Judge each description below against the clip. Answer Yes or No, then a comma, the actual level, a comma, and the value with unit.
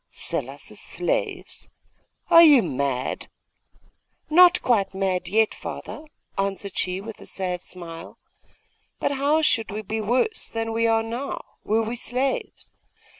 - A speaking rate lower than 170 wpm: Yes, average, 140 wpm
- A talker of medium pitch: No, high, 225 Hz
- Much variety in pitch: Yes, wide, 5.9 semitones